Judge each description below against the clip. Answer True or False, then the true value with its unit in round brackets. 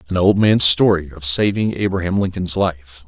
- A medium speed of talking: True (175 wpm)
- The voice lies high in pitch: False (90 Hz)